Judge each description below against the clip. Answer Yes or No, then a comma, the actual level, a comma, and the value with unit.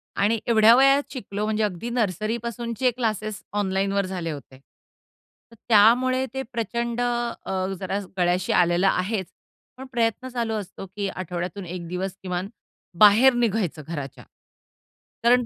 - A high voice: Yes, high, 210 Hz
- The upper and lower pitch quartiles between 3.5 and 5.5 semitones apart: Yes, average, 4.1 semitones